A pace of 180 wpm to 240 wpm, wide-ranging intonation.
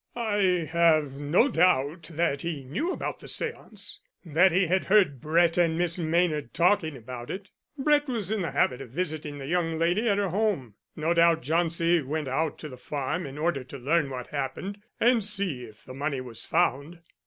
No: average, 190 wpm; average, 4.5 semitones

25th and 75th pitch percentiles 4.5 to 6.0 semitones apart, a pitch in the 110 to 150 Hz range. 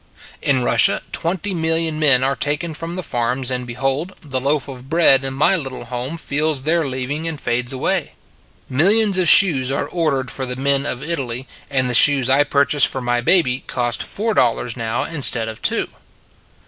No: average, 4.1 semitones; medium, 140 Hz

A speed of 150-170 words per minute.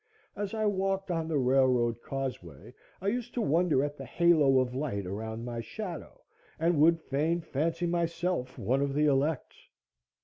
Yes: average, 165 wpm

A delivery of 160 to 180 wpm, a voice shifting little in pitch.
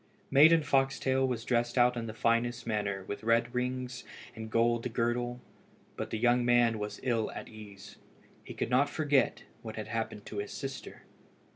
Yes: average, 175 wpm; narrow, 2.2 semitones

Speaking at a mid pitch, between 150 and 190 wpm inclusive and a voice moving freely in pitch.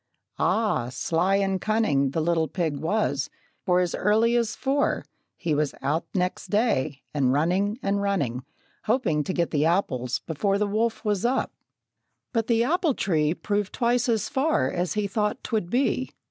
No: high, 195 Hz; average, 160 wpm; wide, 5.8 semitones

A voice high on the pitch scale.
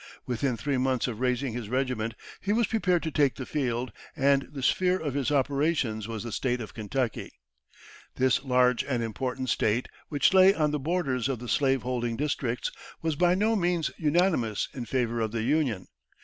No: low, 130 Hz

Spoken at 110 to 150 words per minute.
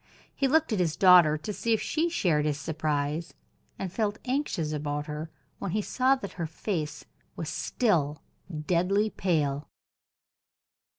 Yes: average, 145 wpm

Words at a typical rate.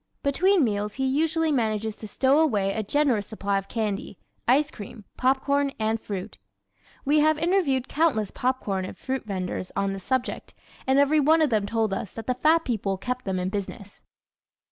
Yes: average, 180 wpm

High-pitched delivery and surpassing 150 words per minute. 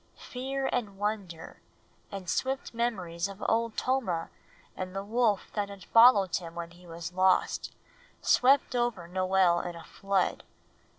No: high, 195 Hz; average, 140 wpm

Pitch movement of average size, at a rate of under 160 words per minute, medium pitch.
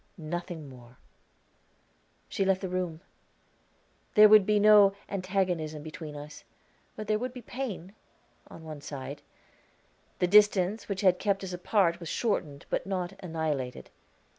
Yes: average, 4.4 semitones; average, 140 wpm; medium, 180 Hz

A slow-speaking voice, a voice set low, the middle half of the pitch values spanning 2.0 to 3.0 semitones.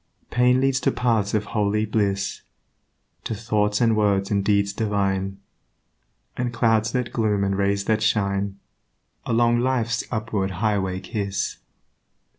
Yes: slow, 130 wpm; low, 105 Hz; narrow, 2.6 semitones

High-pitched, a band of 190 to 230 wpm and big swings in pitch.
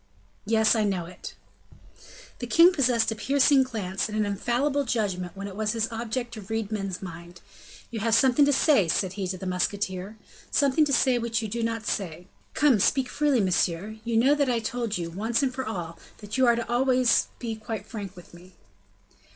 No: high, 220 Hz; average, 200 wpm; average, 4.3 semitones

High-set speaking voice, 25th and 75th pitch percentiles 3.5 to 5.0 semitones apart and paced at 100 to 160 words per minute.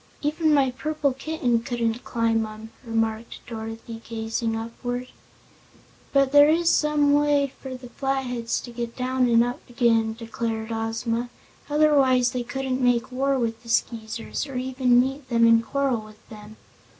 No: high, 245 Hz; average, 2.9 semitones; average, 150 wpm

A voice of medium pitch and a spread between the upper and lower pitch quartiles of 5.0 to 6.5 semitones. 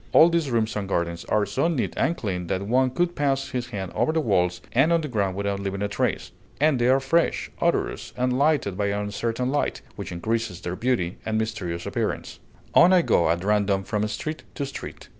No: low, 110 Hz; wide, 5.6 semitones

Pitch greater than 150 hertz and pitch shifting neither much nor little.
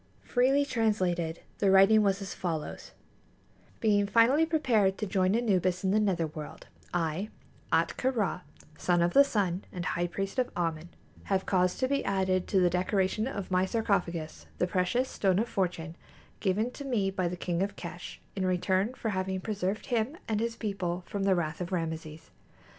Yes: high, 190 Hz; average, 3.4 semitones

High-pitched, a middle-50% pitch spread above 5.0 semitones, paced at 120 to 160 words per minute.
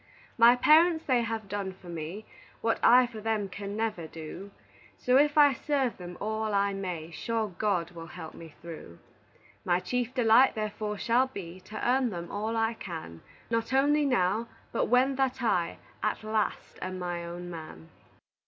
No: high, 215 Hz; wide, 5.5 semitones; average, 170 wpm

